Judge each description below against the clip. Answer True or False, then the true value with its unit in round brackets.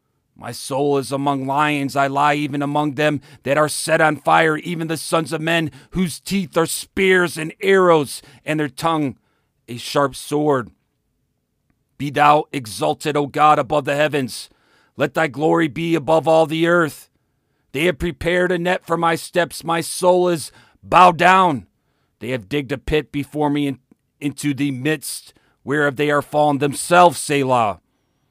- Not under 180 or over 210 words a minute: False (165 wpm)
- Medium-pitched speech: True (150 Hz)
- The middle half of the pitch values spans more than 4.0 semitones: False (2.8 semitones)